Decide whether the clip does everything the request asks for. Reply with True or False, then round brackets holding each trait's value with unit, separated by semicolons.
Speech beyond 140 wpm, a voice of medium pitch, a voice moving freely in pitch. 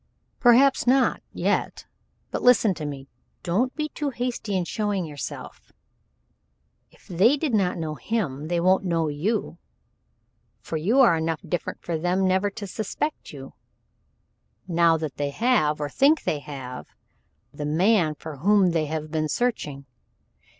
True (150 wpm; 175 Hz; 6.5 semitones)